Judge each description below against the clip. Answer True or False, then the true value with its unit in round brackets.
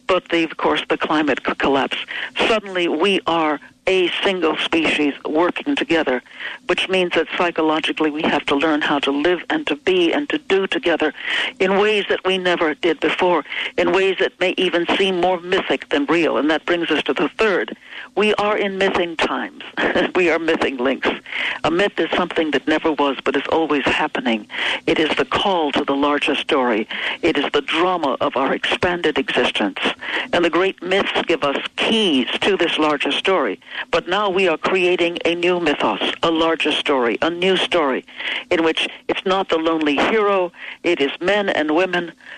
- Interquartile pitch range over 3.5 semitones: False (3.2 semitones)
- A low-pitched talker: False (175 Hz)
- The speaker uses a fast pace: False (185 wpm)